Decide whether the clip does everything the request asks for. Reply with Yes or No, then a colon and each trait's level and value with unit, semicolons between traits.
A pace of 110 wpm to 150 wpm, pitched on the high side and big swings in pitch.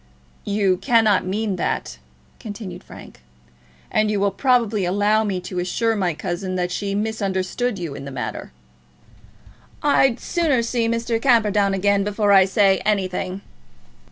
No: average, 140 wpm; high, 205 Hz; average, 3.1 semitones